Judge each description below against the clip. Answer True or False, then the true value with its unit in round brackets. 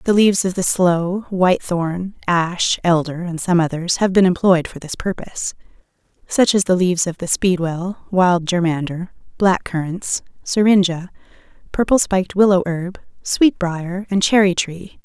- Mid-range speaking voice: True (180 Hz)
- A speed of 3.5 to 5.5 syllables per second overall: True (4.5 syllables/s)